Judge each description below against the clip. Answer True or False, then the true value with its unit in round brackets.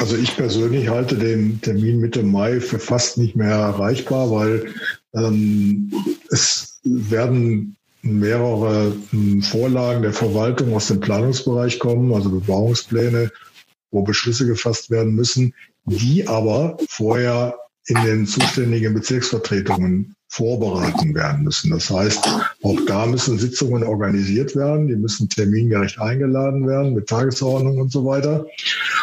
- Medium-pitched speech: False (115 Hz)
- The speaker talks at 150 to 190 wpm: False (125 wpm)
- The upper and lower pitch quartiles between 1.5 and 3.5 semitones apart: True (2.9 semitones)